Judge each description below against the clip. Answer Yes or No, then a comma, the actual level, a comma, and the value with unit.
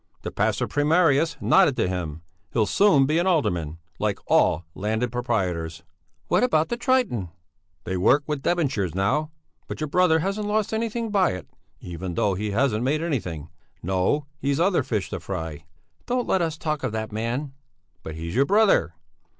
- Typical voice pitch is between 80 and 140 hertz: Yes, low, 135 Hz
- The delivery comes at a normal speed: Yes, average, 170 wpm